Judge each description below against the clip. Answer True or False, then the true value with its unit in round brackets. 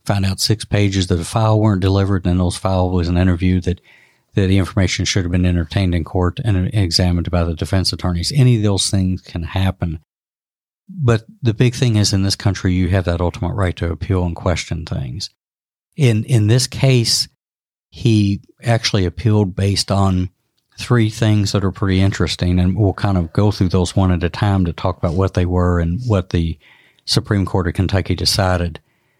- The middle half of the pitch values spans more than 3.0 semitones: False (2.7 semitones)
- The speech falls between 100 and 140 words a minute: False (195 wpm)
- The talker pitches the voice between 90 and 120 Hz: True (95 Hz)